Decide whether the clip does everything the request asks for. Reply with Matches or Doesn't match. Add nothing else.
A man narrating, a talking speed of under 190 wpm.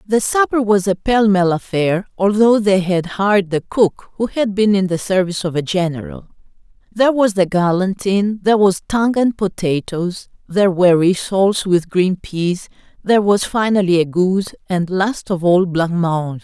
Doesn't match